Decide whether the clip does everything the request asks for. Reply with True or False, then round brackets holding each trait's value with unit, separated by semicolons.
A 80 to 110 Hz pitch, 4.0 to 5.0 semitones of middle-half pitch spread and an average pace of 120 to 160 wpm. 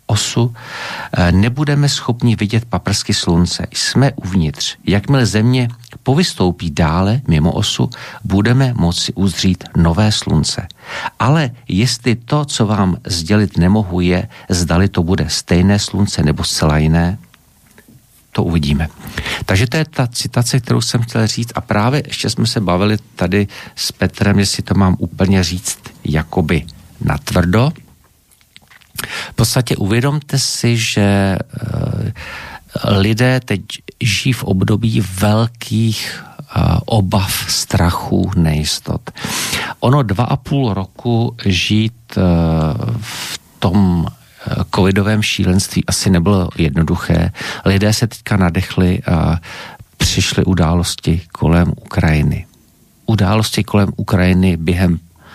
False (100 Hz; 4.6 semitones; 110 wpm)